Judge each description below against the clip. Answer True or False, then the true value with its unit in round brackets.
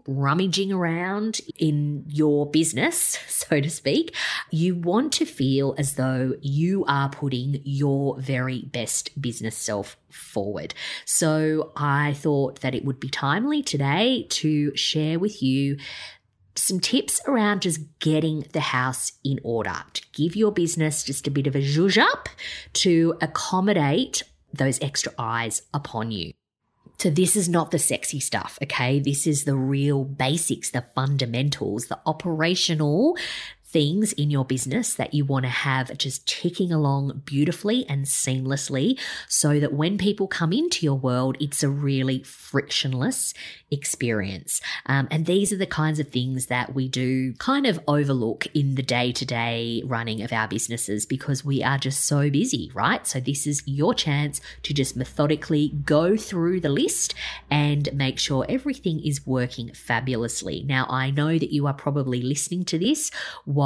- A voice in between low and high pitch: True (145 Hz)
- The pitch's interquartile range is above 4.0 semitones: False (3.5 semitones)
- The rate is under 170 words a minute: True (160 wpm)